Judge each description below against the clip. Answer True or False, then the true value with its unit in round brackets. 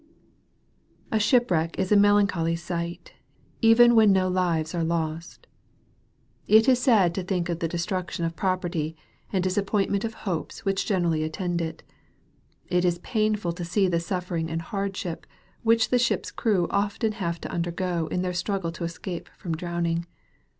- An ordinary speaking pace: True (155 wpm)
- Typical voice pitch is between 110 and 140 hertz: False (180 Hz)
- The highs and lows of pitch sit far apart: False (3.2 semitones)